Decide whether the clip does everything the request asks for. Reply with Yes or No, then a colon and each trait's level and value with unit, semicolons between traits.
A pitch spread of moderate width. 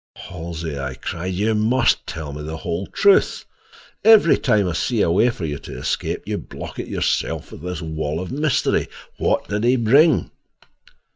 No: wide, 6.9 semitones